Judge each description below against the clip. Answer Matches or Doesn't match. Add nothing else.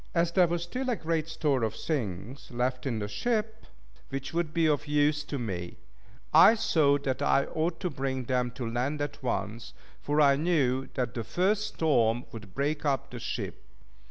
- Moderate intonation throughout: Matches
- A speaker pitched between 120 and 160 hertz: Matches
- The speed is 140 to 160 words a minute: Doesn't match